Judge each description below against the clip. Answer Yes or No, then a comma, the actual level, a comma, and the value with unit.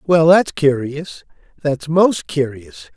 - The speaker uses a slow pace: Yes, slow, 100 wpm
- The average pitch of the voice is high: No, medium, 155 Hz